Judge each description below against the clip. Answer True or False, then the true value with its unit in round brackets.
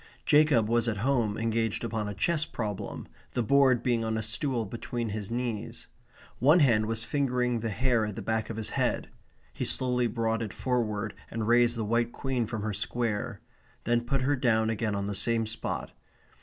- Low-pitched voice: True (115 Hz)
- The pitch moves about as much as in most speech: False (2.1 semitones)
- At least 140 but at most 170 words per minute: False (190 wpm)